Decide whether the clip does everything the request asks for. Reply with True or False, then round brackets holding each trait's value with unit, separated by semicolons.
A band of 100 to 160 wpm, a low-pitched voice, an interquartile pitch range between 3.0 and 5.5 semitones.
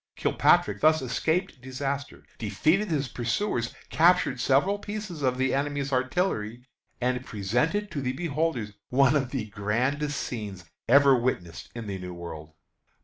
True (140 wpm; 130 Hz; 4.6 semitones)